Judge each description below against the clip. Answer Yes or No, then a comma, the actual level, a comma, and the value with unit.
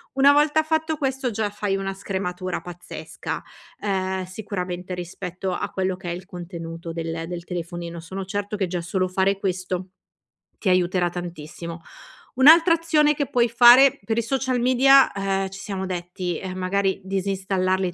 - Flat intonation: No, average, 4.1 semitones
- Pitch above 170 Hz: Yes, high, 190 Hz